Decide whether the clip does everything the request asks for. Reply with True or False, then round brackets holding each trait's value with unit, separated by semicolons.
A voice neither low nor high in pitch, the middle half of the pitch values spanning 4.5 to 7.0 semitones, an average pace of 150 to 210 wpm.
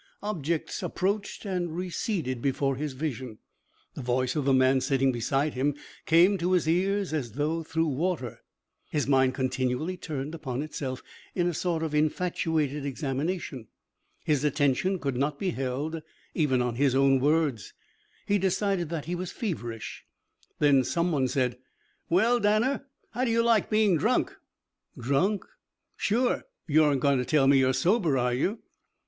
True (150 Hz; 5.2 semitones; 155 wpm)